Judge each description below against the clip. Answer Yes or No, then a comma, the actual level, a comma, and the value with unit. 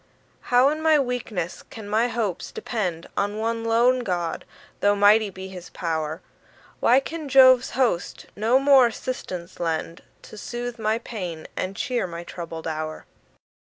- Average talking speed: Yes, average, 150 wpm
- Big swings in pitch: Yes, wide, 5.8 semitones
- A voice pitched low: No, high, 215 Hz